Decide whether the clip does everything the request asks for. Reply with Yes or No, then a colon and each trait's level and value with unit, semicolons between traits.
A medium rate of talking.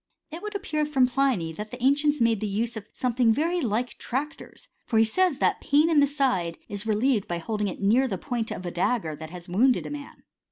No: fast, 225 wpm